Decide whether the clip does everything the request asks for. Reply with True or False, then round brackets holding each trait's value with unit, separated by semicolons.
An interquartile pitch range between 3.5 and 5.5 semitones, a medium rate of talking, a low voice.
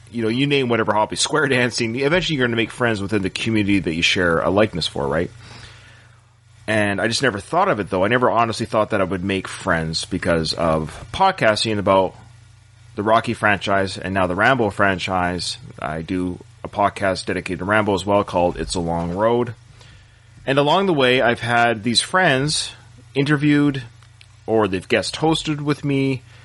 True (3.8 semitones; 185 wpm; 110 Hz)